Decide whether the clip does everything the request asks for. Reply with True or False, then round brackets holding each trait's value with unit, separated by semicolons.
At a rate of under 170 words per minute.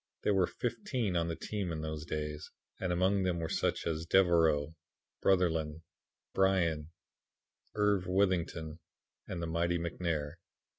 True (140 wpm)